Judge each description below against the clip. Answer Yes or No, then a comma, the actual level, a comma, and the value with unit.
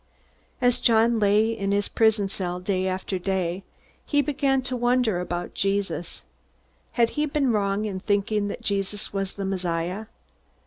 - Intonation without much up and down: No, average, 3.3 semitones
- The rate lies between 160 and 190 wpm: No, average, 150 wpm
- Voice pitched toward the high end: Yes, high, 200 Hz